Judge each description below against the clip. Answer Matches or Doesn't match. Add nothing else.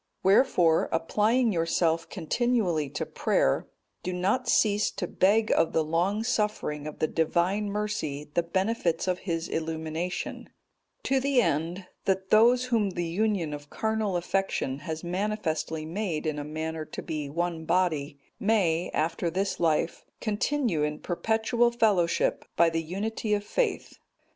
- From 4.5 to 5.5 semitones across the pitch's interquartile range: Matches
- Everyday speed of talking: Matches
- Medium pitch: Matches